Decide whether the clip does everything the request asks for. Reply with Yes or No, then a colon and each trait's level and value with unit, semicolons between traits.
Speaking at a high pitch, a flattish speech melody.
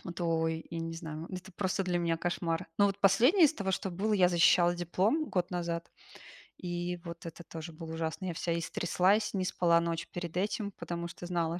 No: medium, 175 Hz; narrow, 2.0 semitones